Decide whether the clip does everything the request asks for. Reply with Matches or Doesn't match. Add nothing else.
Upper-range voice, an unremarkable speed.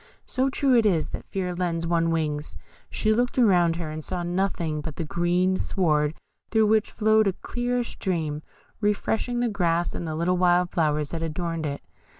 Doesn't match